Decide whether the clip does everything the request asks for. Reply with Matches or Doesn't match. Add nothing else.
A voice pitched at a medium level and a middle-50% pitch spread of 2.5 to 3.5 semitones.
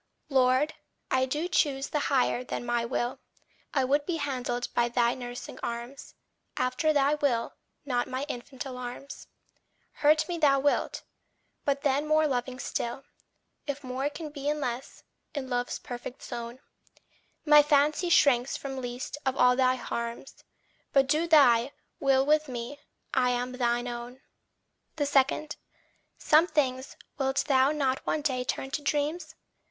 Doesn't match